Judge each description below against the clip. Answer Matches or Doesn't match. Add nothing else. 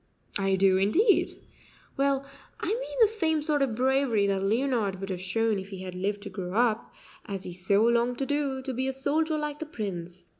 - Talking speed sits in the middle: Doesn't match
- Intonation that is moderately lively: Doesn't match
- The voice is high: Matches